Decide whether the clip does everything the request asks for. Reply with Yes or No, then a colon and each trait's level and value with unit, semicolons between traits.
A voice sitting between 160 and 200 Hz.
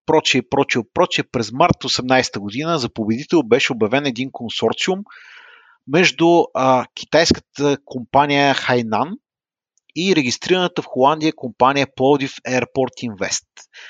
No: low, 135 Hz